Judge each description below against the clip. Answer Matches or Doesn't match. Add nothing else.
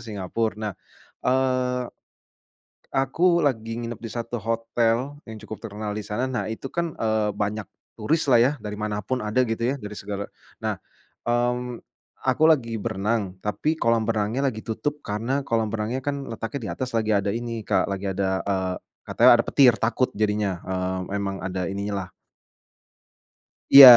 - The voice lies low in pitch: Matches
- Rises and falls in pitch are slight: Doesn't match